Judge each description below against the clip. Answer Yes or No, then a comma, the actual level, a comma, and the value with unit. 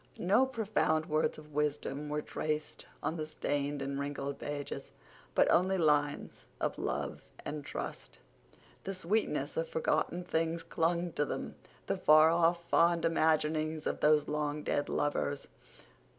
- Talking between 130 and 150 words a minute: Yes, slow, 135 wpm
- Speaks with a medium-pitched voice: Yes, medium, 155 Hz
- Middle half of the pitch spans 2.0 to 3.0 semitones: Yes, narrow, 2.6 semitones